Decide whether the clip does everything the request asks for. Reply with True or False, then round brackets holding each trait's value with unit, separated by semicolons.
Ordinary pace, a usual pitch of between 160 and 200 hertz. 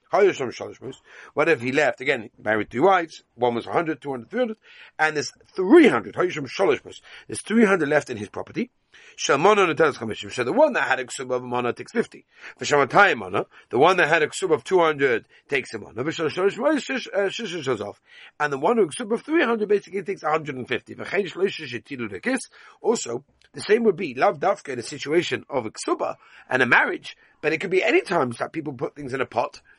True (175 wpm; 185 Hz)